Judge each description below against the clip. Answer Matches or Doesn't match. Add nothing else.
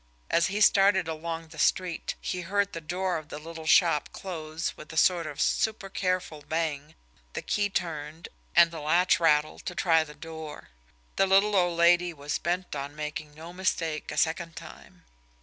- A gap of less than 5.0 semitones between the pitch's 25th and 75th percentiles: Matches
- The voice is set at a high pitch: Doesn't match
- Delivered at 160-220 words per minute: Matches